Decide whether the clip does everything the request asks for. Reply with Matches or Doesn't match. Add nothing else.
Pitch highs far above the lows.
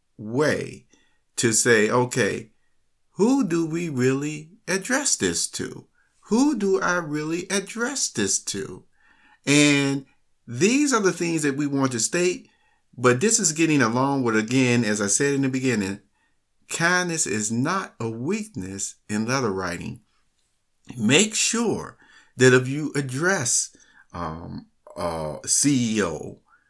Matches